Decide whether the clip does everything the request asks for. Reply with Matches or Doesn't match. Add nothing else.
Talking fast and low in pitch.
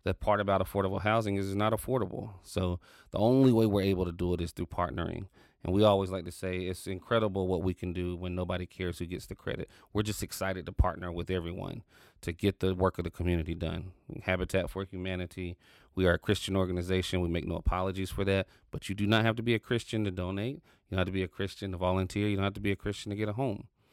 Matches